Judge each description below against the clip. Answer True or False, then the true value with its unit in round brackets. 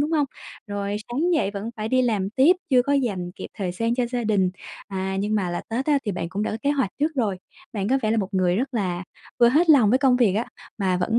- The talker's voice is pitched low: False (220 Hz)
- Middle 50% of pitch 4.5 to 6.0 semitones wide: True (5.0 semitones)